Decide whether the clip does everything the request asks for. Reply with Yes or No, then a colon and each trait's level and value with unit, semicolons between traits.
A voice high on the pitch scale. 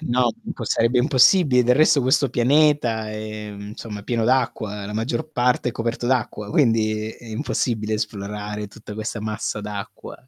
No: low, 115 Hz